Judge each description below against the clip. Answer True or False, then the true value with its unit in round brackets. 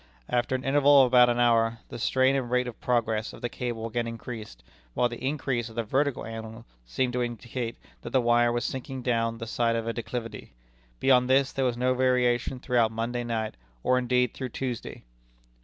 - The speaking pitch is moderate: False (120 Hz)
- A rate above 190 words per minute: True (200 wpm)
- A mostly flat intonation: True (1.7 semitones)